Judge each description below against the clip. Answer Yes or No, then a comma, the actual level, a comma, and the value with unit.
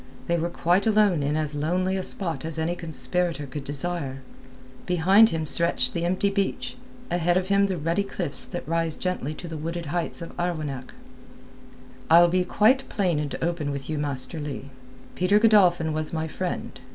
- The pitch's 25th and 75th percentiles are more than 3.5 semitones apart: No, average, 3.1 semitones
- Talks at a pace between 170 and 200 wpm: Yes, average, 175 wpm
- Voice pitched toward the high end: No, medium, 170 Hz